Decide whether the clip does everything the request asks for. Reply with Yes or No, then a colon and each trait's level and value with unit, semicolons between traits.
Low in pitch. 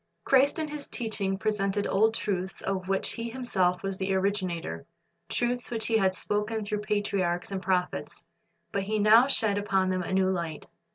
No: high, 200 Hz